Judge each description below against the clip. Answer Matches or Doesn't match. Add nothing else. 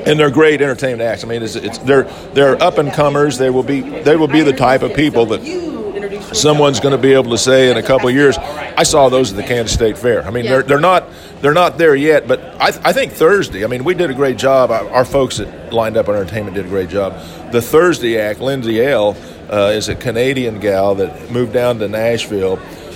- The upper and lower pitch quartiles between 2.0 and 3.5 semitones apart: Doesn't match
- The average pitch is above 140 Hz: Doesn't match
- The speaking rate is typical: Doesn't match